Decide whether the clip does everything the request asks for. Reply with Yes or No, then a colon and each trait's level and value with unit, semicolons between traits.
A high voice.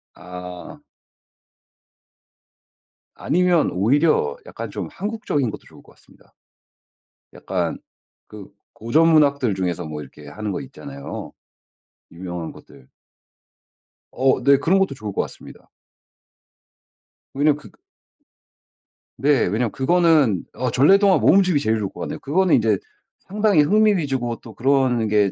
No: low, 130 Hz